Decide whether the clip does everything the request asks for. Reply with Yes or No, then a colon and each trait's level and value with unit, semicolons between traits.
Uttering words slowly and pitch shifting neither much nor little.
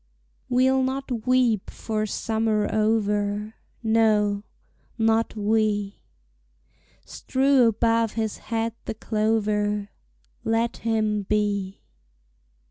No: slow, 85 wpm; narrow, 1.6 semitones